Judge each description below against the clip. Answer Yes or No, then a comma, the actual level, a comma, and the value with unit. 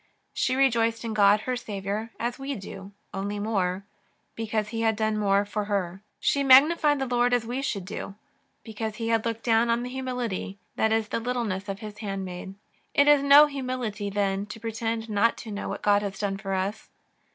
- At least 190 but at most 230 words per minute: Yes, average, 195 wpm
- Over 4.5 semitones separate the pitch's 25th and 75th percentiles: No, average, 3.2 semitones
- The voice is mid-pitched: No, high, 220 Hz